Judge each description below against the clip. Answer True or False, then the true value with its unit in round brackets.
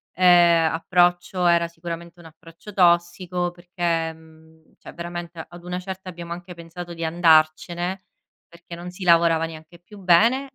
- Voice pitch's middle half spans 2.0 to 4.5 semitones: False (1.2 semitones)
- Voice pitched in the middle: True (170 Hz)